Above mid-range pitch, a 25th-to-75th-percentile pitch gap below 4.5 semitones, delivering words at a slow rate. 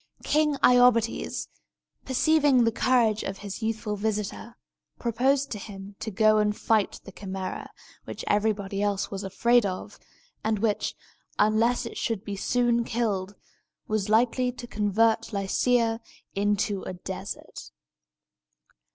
Yes: high, 215 Hz; average, 2.8 semitones; slow, 125 wpm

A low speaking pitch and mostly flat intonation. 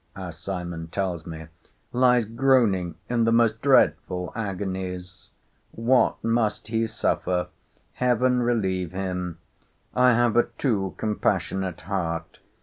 No: low, 100 Hz; average, 4.6 semitones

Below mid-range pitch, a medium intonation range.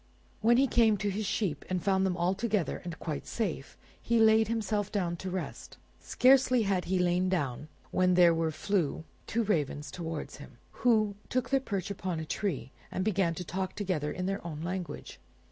No: high, 190 Hz; average, 3.9 semitones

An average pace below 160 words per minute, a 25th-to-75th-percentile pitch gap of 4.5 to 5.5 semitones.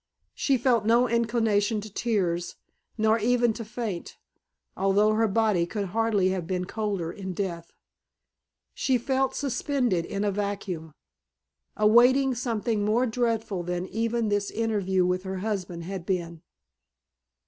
No: slow, 135 wpm; average, 3.7 semitones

